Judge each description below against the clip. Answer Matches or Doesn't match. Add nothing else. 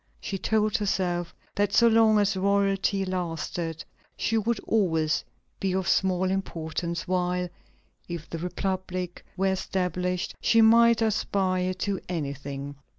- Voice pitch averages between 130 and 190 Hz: Matches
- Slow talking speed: Matches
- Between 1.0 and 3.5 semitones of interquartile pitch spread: Matches